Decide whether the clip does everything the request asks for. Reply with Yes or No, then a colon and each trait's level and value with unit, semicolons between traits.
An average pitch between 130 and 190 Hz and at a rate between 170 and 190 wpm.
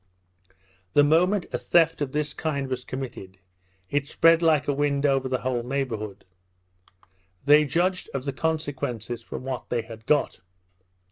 No: medium, 140 Hz; average, 150 wpm